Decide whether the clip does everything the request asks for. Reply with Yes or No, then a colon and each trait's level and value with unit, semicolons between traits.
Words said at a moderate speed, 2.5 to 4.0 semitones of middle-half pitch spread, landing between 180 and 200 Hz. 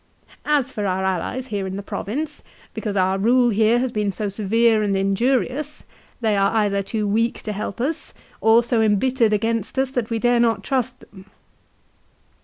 No: average, 185 wpm; average, 3.4 semitones; high, 220 Hz